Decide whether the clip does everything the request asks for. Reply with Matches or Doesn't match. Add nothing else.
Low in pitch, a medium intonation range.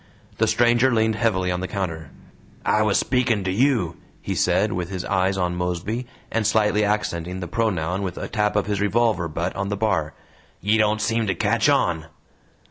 Matches